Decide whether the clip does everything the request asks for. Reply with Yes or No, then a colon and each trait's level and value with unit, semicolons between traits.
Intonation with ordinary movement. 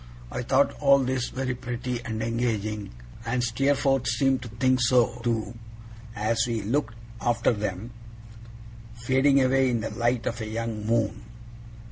No: narrow, 2.2 semitones